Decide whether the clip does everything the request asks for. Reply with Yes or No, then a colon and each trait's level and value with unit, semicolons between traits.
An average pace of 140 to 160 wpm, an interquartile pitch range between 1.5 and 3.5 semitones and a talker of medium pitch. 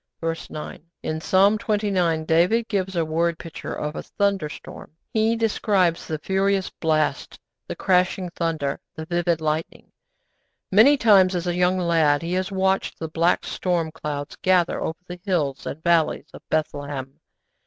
Yes: average, 155 wpm; average, 3.2 semitones; medium, 170 Hz